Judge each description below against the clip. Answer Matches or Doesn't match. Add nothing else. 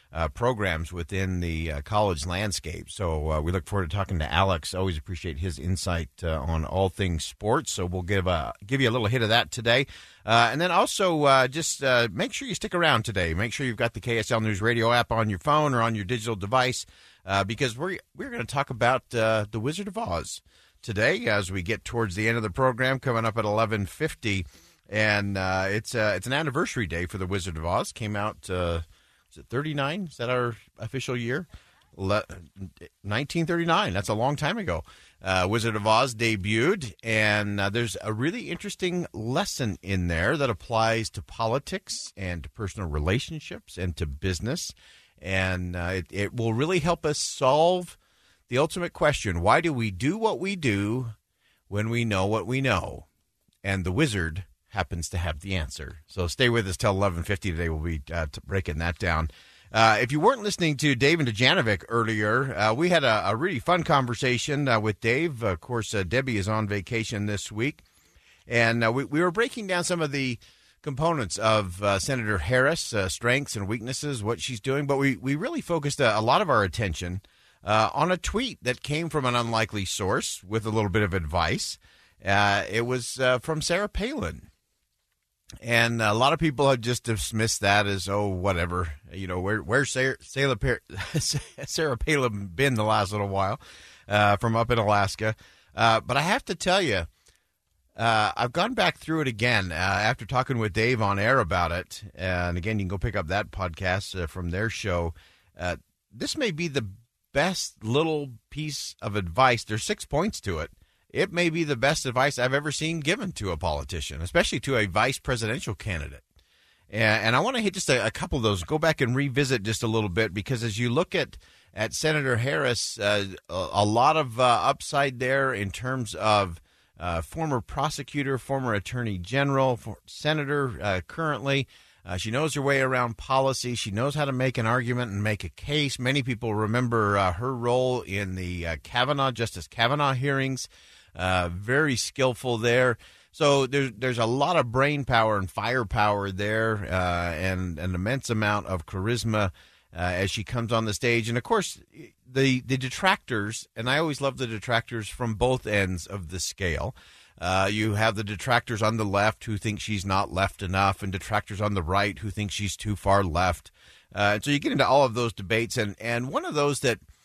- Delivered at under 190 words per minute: Doesn't match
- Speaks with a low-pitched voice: Matches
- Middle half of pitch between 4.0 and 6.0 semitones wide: Matches